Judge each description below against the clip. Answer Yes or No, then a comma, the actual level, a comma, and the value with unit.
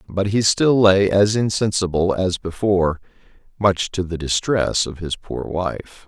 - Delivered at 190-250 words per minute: No, average, 160 wpm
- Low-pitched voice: Yes, very low, 95 Hz